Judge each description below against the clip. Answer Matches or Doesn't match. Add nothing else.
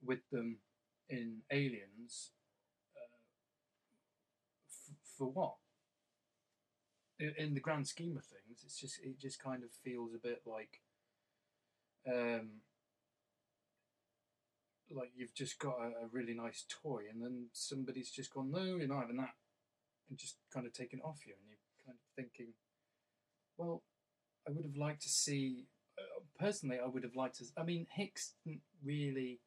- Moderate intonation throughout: Matches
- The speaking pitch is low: Matches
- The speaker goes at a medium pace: Matches